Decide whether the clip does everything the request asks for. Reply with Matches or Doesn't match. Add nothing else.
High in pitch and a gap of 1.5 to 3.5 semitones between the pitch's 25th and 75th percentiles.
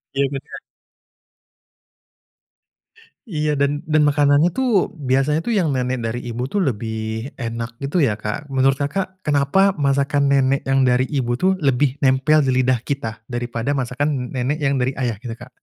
Doesn't match